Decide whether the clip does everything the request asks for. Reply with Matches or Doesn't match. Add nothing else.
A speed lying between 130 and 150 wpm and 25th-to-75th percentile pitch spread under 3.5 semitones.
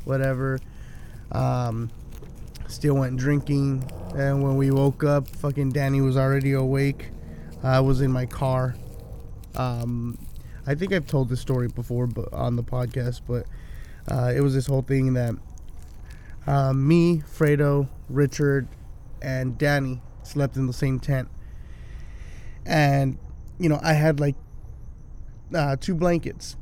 Matches